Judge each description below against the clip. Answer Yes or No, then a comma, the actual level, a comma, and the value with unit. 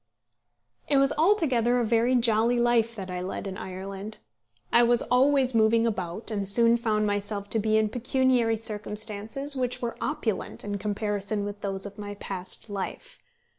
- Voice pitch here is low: No, high, 220 Hz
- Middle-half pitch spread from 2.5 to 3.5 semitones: Yes, average, 2.9 semitones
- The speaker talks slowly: No, average, 165 wpm